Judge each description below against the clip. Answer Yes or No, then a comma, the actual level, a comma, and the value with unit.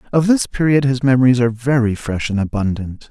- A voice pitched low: Yes, low, 125 Hz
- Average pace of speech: Yes, average, 195 wpm